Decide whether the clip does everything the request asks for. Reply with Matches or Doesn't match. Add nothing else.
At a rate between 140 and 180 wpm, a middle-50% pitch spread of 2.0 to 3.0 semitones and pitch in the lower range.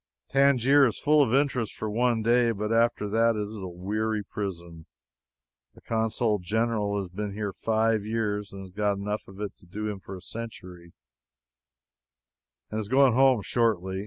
Matches